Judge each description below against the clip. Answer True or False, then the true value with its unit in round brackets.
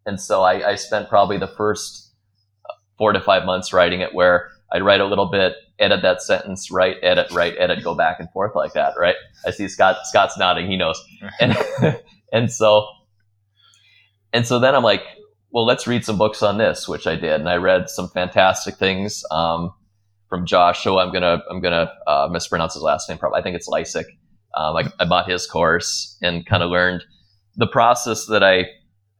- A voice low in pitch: True (100 Hz)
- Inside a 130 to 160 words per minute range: False (200 wpm)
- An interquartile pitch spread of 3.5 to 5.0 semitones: False (2.8 semitones)